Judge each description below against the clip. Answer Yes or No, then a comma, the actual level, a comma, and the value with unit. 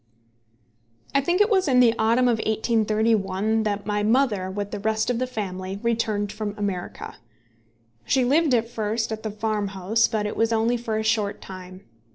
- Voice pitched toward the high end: Yes, high, 220 Hz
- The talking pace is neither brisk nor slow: Yes, average, 180 wpm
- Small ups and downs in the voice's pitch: Yes, narrow, 2.2 semitones